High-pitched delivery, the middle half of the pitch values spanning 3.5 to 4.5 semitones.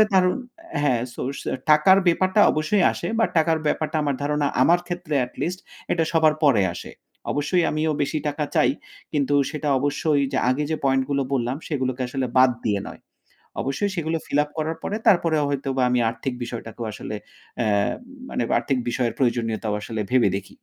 No: medium, 145 Hz; average, 3.8 semitones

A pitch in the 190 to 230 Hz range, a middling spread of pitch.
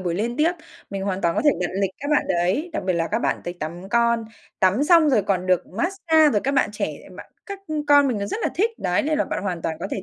No: high, 215 Hz; wide, 8.3 semitones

